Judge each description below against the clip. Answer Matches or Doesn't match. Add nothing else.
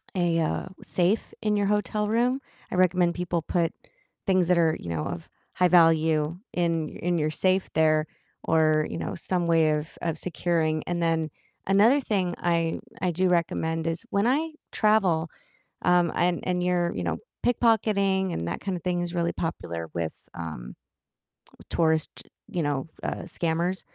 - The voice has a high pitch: Doesn't match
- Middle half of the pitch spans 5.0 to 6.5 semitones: Doesn't match